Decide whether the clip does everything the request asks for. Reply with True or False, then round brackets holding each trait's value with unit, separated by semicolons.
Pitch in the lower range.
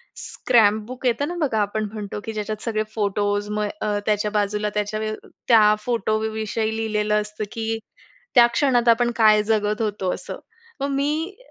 False (215 Hz)